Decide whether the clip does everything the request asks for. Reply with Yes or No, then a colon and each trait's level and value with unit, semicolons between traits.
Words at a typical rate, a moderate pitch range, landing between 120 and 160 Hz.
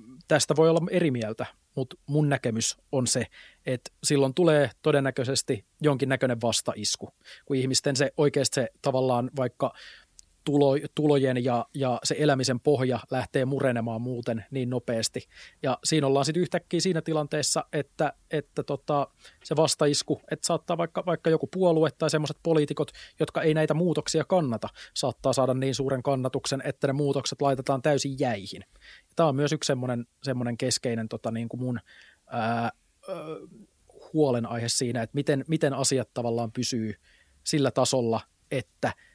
Yes: average, 145 wpm; average, 3.4 semitones; low, 135 Hz